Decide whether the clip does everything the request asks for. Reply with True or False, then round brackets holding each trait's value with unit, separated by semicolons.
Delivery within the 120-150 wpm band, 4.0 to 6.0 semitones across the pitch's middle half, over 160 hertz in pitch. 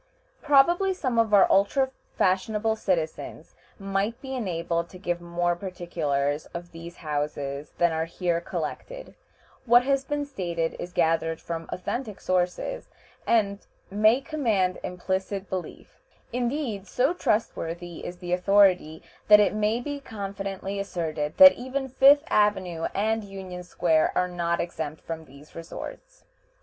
True (135 wpm; 5.0 semitones; 190 Hz)